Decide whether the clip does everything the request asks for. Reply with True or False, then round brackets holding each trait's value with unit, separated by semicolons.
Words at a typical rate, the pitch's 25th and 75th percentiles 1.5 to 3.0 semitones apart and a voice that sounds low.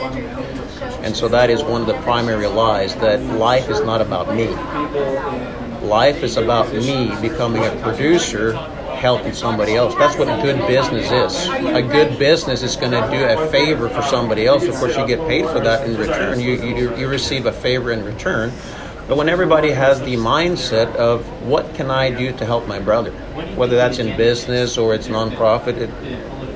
True (190 wpm; 2.7 semitones; 120 Hz)